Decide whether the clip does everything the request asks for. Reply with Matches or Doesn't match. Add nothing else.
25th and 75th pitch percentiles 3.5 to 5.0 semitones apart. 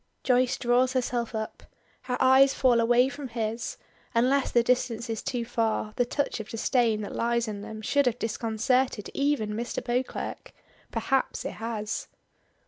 Doesn't match